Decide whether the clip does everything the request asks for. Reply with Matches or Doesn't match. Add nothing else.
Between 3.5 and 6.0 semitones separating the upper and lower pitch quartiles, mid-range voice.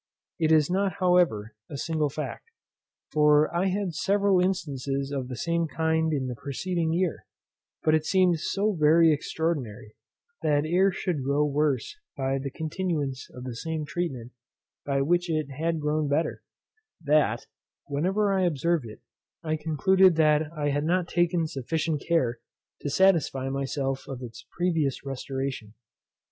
Matches